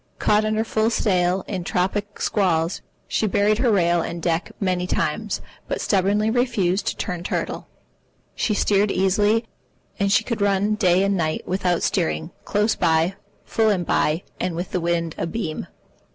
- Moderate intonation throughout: Yes, average, 3.2 semitones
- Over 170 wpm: No, average, 160 wpm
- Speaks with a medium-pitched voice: No, high, 195 Hz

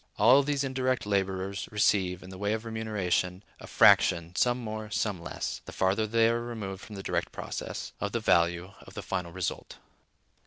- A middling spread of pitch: Yes, average, 3.5 semitones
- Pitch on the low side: Yes, low, 105 Hz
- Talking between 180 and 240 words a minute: Yes, average, 185 wpm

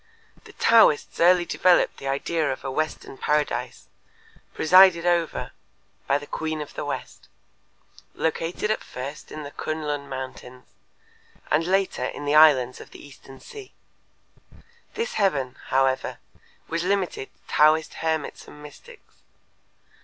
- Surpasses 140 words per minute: No, slow, 135 wpm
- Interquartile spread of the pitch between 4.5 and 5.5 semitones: No, average, 3.9 semitones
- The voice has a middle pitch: Yes, medium, 155 Hz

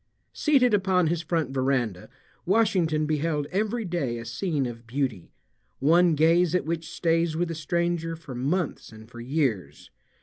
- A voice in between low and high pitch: Yes, medium, 160 Hz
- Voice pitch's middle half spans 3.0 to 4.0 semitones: No, average, 4.6 semitones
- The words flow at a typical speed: Yes, average, 155 wpm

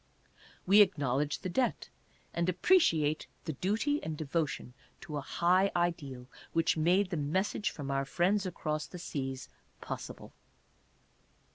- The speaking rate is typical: No, slow, 130 wpm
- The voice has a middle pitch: Yes, medium, 165 Hz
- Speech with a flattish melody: No, average, 4.3 semitones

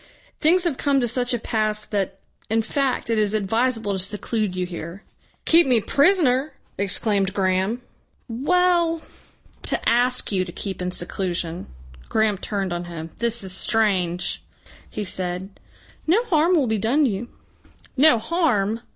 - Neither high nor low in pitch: No, high, 220 Hz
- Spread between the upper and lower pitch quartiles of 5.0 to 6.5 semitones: Yes, wide, 5.4 semitones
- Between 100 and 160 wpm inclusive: Yes, average, 150 wpm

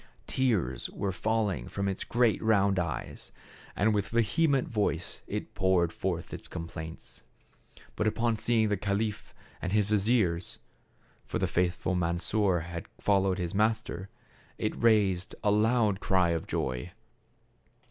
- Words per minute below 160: Yes, average, 145 wpm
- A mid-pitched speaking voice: No, low, 100 Hz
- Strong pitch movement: No, average, 3.7 semitones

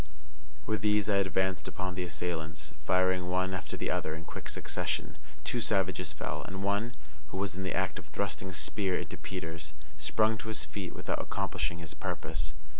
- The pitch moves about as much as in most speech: Yes, average, 3.0 semitones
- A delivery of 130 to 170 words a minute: No, average, 185 wpm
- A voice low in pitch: Yes, very low, 95 Hz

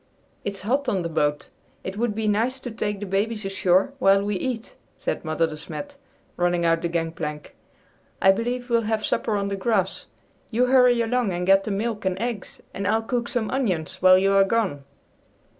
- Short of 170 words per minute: No, average, 195 wpm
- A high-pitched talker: Yes, high, 200 Hz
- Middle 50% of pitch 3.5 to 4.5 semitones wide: Yes, average, 4.0 semitones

